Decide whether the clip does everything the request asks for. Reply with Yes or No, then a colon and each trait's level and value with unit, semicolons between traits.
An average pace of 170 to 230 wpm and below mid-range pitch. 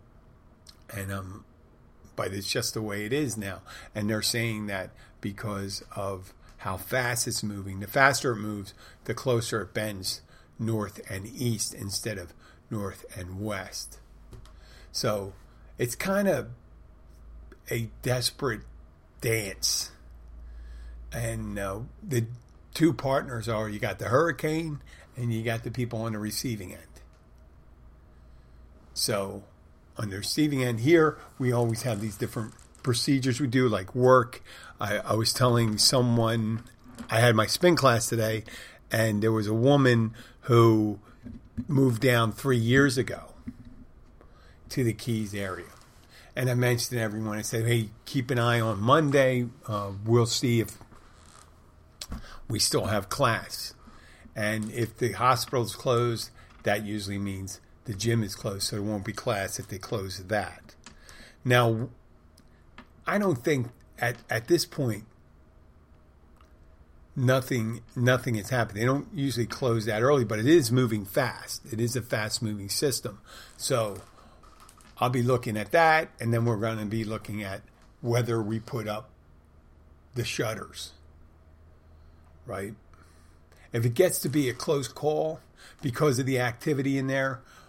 No: average, 145 wpm; low, 110 Hz